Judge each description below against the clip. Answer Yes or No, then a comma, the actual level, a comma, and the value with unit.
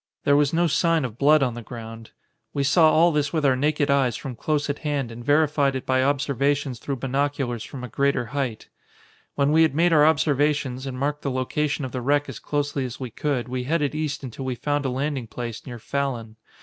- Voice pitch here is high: No, medium, 140 Hz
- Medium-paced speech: No, fast, 220 wpm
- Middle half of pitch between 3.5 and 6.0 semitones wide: No, average, 2.7 semitones